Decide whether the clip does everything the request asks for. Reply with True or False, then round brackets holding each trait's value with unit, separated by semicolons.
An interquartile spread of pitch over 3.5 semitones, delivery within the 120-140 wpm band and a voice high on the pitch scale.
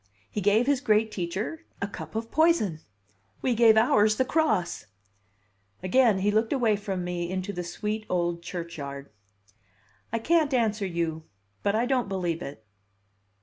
False (4.6 semitones; 150 wpm; 205 Hz)